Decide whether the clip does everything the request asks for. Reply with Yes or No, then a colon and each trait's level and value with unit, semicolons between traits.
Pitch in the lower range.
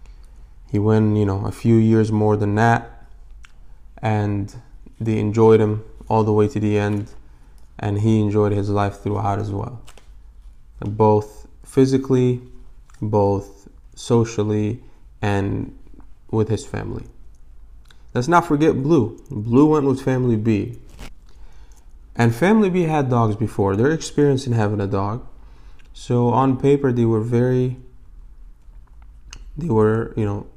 Yes: low, 110 Hz